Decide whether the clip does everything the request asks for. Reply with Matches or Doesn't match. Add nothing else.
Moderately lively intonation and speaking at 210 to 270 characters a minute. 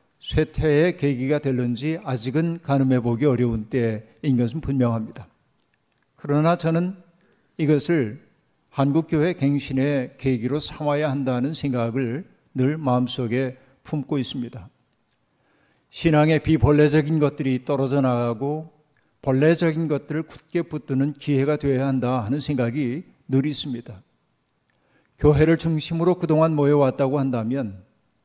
Doesn't match